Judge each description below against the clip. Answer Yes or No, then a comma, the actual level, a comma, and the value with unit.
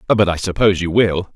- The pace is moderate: No, fast, 220 wpm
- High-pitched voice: No, very low, 95 Hz